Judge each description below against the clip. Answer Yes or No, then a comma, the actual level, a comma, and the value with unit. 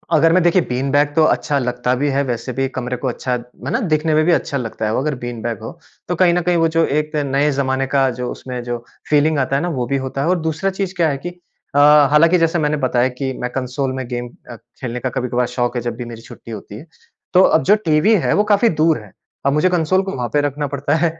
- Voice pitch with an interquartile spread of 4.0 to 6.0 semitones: Yes, average, 4.3 semitones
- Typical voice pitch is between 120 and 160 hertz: Yes, medium, 140 Hz